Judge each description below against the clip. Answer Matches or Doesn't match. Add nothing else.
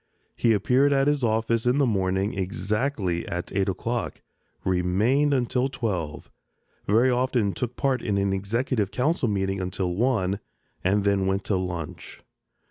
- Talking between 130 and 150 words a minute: Matches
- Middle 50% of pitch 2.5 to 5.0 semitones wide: Matches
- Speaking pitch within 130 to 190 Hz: Doesn't match